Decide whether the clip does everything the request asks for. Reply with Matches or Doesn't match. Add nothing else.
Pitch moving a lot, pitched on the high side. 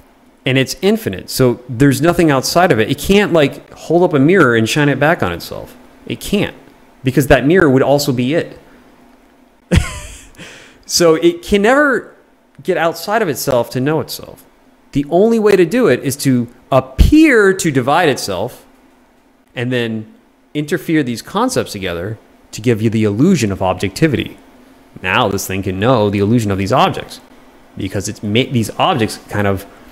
Doesn't match